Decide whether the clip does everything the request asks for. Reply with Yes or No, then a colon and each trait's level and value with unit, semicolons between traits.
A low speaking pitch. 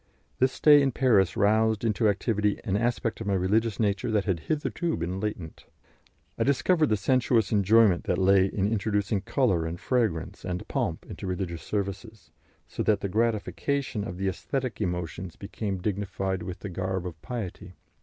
Yes: low, 100 Hz